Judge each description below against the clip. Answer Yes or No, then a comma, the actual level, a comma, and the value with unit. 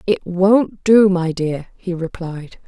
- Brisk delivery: No, average, 155 wpm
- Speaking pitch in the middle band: Yes, medium, 180 Hz